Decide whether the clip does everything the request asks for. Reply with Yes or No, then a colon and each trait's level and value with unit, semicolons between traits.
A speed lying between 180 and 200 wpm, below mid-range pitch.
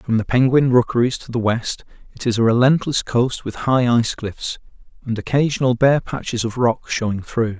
Yes: average, 190 wpm; low, 120 Hz